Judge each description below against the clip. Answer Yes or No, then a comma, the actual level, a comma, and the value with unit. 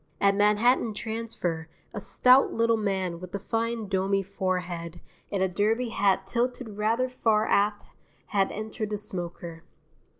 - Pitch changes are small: No, average, 3.0 semitones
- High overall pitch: Yes, high, 205 Hz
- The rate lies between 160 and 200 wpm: No, average, 140 wpm